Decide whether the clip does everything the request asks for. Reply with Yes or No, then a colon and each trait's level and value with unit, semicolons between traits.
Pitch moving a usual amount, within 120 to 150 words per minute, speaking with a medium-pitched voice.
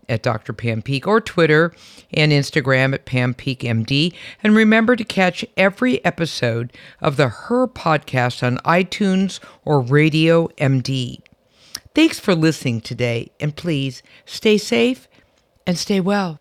No: wide, 6.5 semitones; average, 140 wpm; medium, 155 Hz